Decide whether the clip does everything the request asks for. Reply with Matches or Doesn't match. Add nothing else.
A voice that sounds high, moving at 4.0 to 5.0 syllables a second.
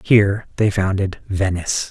Doesn't match